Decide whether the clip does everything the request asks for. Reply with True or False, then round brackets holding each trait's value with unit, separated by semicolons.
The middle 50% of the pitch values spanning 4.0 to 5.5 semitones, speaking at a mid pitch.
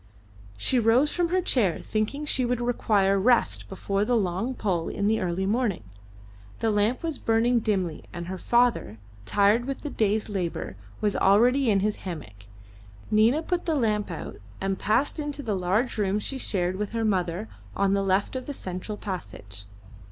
False (4.4 semitones; 210 Hz)